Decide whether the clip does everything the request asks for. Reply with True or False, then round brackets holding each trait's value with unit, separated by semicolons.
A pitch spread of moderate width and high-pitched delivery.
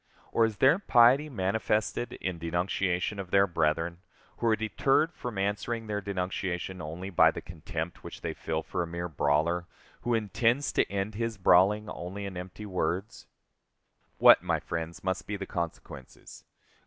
False (3.8 semitones; 95 Hz)